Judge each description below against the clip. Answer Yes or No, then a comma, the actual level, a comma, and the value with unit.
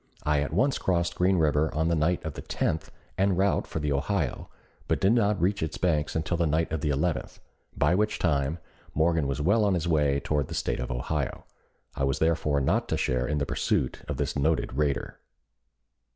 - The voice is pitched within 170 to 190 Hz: No, very low, 80 Hz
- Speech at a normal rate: No, fast, 210 wpm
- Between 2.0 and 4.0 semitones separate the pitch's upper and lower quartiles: Yes, average, 3.4 semitones